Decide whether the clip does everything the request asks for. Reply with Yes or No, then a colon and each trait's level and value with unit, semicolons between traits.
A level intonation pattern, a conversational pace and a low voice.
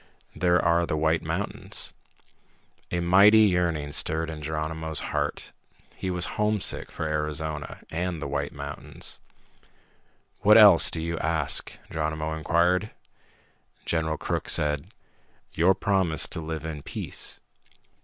No: narrow, 2.3 semitones; slow, 125 wpm; very low, 80 Hz